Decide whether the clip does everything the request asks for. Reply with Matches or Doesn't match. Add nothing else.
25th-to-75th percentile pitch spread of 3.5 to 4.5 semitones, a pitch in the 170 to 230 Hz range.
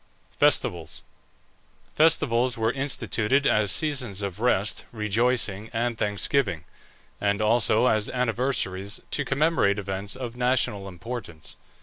Doesn't match